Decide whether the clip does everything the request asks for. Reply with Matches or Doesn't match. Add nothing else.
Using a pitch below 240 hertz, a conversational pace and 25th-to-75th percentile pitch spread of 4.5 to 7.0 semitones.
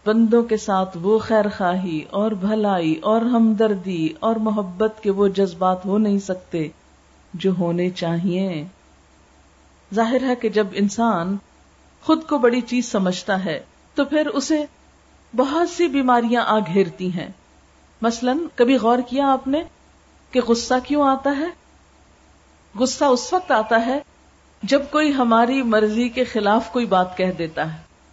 Matches